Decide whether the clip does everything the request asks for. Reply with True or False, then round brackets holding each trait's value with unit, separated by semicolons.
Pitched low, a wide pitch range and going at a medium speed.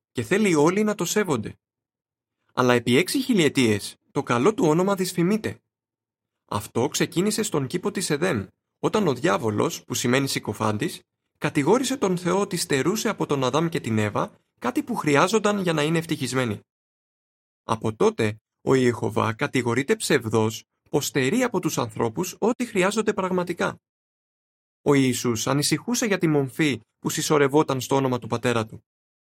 False (145 Hz; 7.2 semitones; 145 wpm)